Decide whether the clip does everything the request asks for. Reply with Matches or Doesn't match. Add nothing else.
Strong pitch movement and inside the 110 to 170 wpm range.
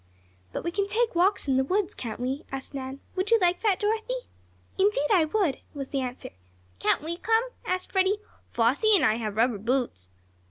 Doesn't match